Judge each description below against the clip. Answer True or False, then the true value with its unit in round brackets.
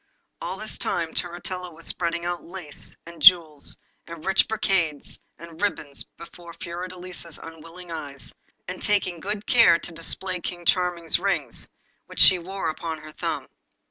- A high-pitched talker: False (175 Hz)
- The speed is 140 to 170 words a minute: True (145 wpm)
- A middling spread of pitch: False (2.0 semitones)